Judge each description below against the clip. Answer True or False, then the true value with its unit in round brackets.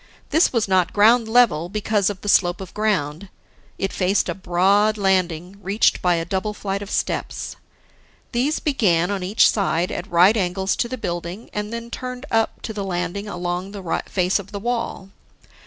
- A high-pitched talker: True (195 Hz)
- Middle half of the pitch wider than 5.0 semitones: False (3.2 semitones)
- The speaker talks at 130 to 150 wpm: False (180 wpm)